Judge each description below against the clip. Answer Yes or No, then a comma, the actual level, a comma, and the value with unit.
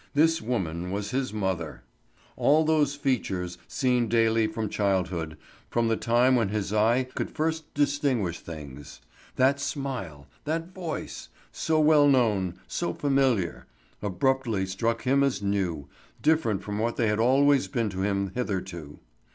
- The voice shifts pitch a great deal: Yes, wide, 6.3 semitones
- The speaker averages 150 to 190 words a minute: No, slow, 135 wpm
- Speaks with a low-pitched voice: Yes, low, 115 Hz